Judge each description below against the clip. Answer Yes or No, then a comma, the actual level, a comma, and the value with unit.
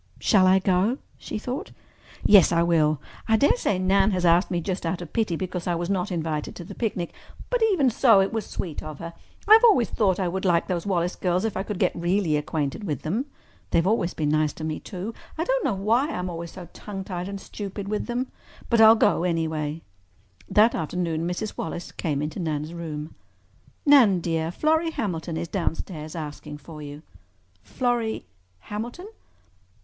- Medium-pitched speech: Yes, medium, 180 Hz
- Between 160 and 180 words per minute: No, average, 190 wpm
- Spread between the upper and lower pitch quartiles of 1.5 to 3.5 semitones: No, average, 4.6 semitones